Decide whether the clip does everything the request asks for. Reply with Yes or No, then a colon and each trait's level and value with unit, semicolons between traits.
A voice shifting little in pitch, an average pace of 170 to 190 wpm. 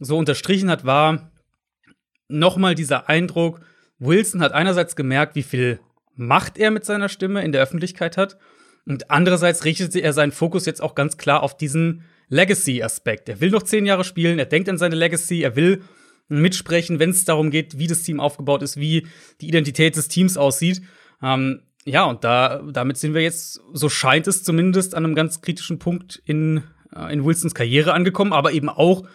No: average, 3.4 semitones; average, 185 wpm